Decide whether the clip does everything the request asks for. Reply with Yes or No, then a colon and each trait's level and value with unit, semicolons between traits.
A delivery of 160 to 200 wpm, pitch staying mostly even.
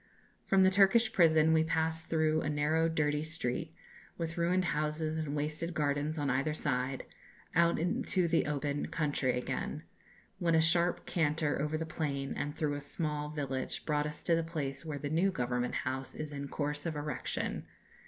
Yes: average, 175 wpm; narrow, 2.0 semitones